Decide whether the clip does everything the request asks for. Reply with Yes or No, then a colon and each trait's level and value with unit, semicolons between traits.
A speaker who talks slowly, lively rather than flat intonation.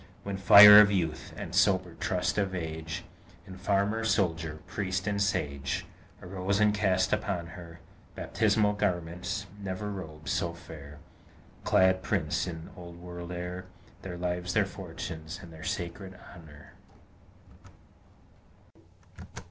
No: slow, 125 wpm; average, 2.9 semitones